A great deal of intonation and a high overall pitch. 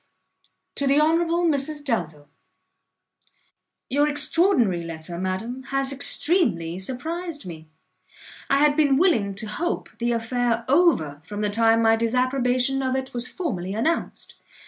Yes: wide, 6.2 semitones; very high, 255 Hz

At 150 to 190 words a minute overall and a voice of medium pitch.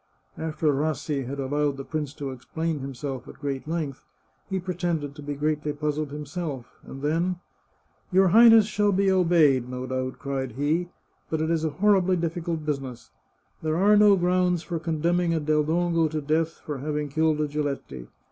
Yes: average, 185 wpm; medium, 155 Hz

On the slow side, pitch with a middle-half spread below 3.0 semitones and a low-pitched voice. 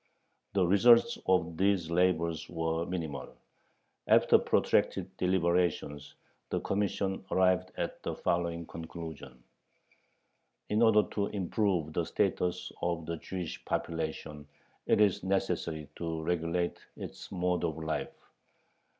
Yes: slow, 115 wpm; narrow, 2.4 semitones; very low, 85 Hz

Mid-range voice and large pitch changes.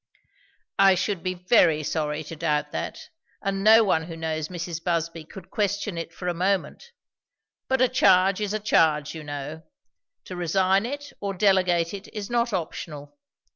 No: medium, 180 Hz; average, 3.6 semitones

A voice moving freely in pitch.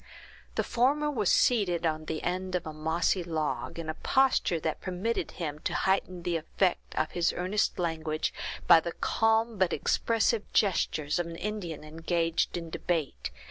No: average, 3.9 semitones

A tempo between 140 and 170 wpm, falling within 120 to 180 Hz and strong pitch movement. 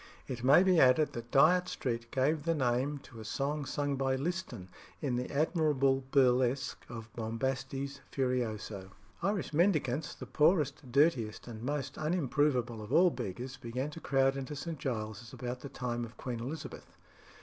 No: average, 160 wpm; low, 135 Hz; average, 3.6 semitones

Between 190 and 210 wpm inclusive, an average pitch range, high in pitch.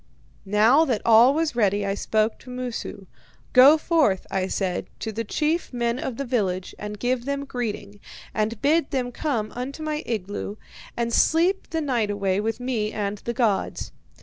No: average, 175 wpm; average, 4.8 semitones; high, 235 Hz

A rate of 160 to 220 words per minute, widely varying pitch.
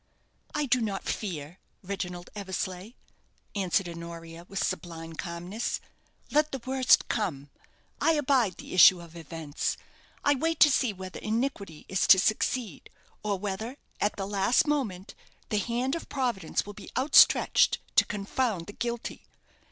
No: average, 145 wpm; wide, 5.7 semitones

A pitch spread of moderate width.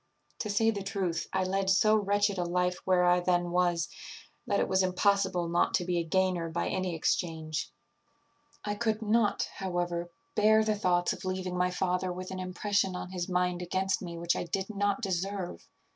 No: narrow, 2.0 semitones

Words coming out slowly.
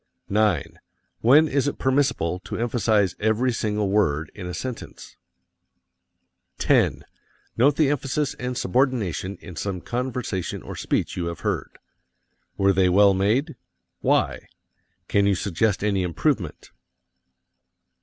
Yes: slow, 125 wpm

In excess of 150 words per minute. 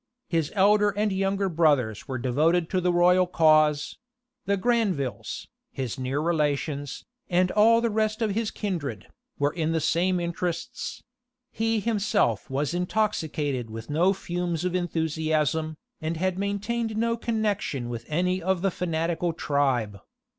No: average, 140 wpm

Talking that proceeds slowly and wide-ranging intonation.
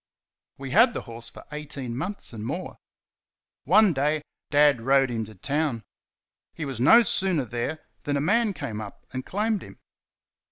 No: average, 165 wpm; wide, 6.7 semitones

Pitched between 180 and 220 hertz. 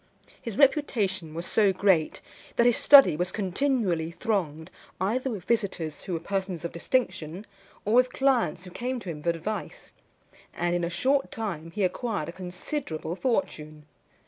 Yes: high, 190 Hz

